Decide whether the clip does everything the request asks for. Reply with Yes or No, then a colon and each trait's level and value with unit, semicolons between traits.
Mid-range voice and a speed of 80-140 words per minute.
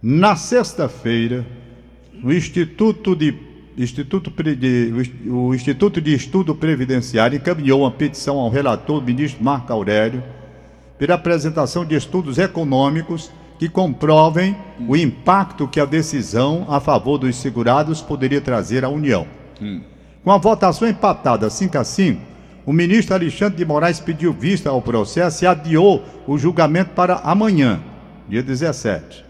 Yes: medium, 150 Hz; average, 130 wpm